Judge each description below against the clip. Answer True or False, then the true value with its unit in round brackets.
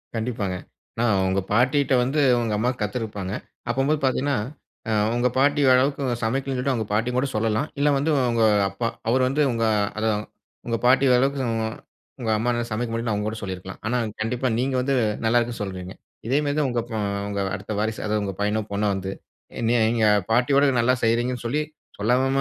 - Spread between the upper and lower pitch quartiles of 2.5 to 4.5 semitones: True (3.3 semitones)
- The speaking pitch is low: True (120 Hz)